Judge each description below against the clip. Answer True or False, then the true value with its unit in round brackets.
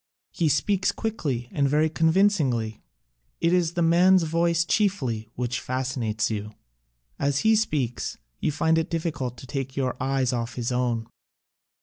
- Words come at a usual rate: True (150 wpm)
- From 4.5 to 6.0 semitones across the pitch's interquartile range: True (5.4 semitones)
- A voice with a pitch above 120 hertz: True (140 Hz)